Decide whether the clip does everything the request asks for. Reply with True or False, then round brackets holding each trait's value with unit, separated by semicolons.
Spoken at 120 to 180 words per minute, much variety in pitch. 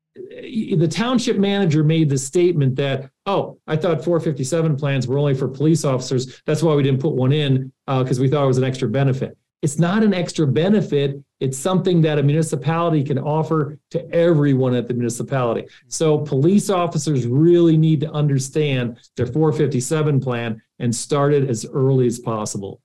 False (175 wpm; 3.6 semitones)